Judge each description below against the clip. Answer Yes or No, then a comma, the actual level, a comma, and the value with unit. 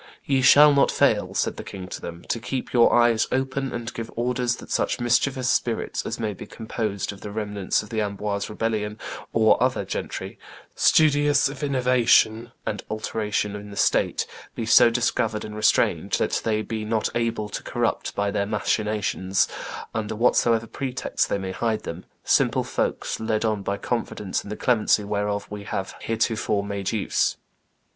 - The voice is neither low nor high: No, low, 110 Hz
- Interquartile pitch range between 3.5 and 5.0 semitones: No, narrow, 2.5 semitones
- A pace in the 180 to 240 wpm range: No, average, 170 wpm